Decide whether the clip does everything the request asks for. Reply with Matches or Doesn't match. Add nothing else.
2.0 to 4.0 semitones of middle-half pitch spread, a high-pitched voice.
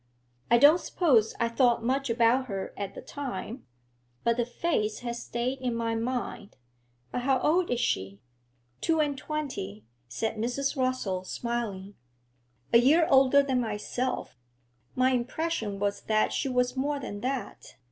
Matches